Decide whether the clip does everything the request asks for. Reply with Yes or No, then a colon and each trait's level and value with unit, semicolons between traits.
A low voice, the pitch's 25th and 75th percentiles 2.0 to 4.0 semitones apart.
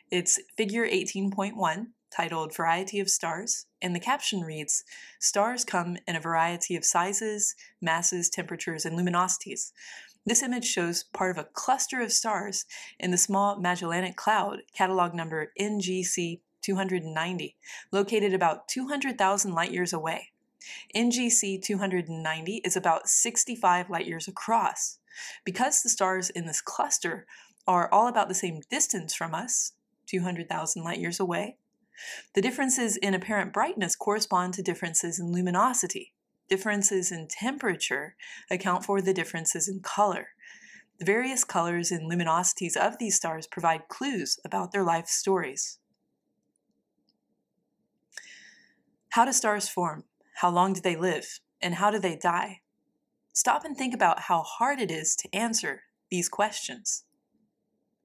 No: high, 190 Hz; average, 3.3 semitones